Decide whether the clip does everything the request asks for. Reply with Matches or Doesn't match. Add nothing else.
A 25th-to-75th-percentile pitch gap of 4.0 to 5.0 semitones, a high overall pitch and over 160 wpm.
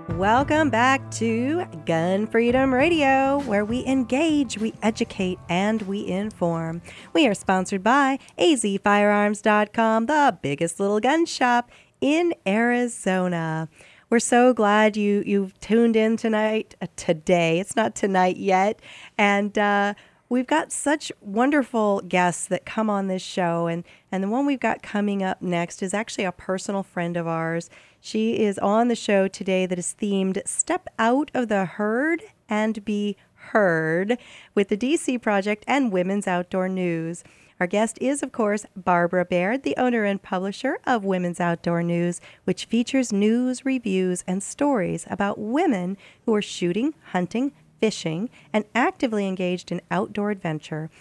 Doesn't match